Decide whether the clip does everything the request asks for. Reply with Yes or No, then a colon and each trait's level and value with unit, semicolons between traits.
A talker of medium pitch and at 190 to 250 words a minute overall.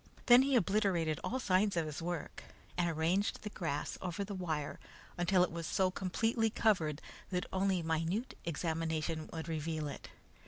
No: medium, 175 Hz; average, 160 wpm